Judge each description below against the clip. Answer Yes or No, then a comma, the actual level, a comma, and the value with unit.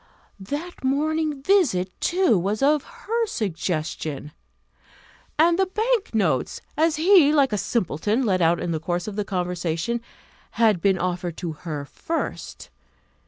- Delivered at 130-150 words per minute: Yes, average, 140 wpm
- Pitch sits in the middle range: No, high, 215 Hz